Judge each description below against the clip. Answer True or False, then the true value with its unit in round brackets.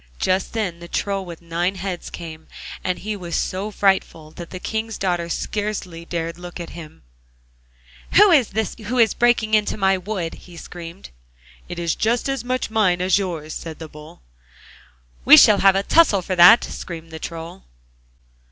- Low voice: False (185 Hz)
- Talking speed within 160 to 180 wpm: True (170 wpm)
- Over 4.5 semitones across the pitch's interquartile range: False (3.9 semitones)